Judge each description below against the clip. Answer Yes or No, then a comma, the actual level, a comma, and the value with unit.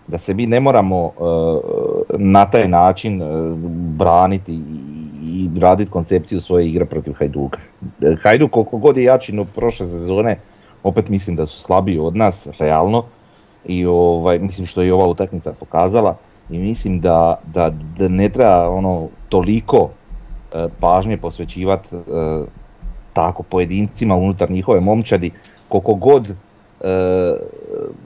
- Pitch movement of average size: Yes, average, 3.5 semitones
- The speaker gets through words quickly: No, average, 140 wpm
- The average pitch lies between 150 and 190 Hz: No, very low, 95 Hz